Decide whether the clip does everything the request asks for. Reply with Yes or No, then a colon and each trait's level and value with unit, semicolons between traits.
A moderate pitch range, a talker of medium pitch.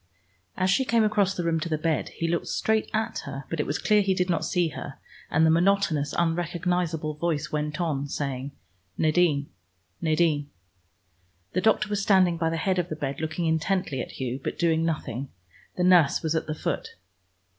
Yes: average, 3.1 semitones; medium, 165 Hz